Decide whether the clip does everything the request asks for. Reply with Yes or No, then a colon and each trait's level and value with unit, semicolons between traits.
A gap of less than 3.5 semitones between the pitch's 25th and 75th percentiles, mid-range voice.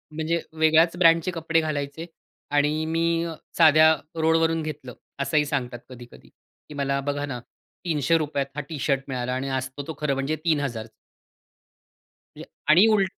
Yes: average, 2.9 semitones; medium, 150 Hz